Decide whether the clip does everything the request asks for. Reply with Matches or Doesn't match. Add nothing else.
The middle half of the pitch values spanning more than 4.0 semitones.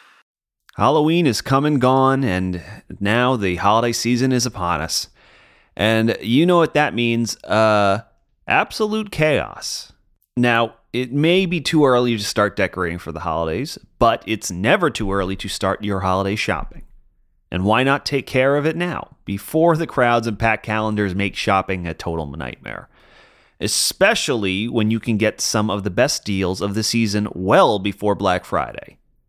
Matches